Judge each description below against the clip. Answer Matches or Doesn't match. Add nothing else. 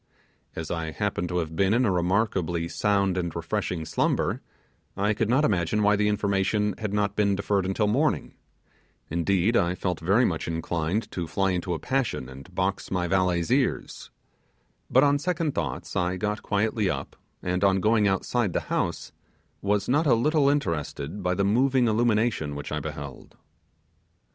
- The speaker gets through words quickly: Doesn't match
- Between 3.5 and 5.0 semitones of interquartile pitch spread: Matches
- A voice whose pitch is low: Matches